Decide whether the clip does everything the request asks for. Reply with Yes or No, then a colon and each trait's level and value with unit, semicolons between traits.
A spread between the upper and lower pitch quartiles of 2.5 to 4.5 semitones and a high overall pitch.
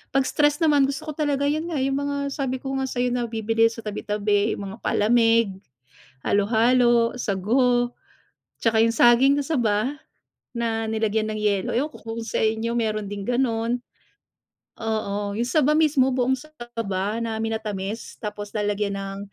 Yes: average, 3.7 semitones; high, 230 Hz